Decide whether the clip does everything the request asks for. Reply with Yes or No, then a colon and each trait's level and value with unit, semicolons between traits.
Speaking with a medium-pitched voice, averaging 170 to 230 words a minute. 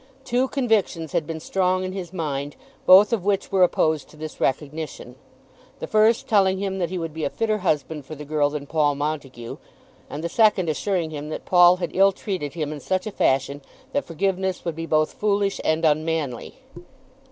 Yes: medium, 165 Hz; average, 195 wpm